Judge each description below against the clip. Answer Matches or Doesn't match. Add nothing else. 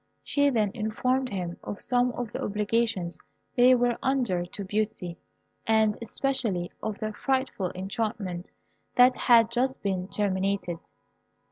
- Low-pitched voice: Doesn't match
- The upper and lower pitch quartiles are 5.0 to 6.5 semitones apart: Doesn't match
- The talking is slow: Matches